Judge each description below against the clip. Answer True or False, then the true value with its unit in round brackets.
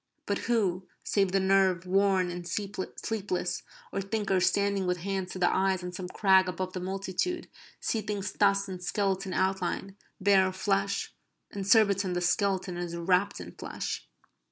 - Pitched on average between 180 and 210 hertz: True (190 Hz)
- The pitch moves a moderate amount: False (1.5 semitones)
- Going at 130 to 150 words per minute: False (160 wpm)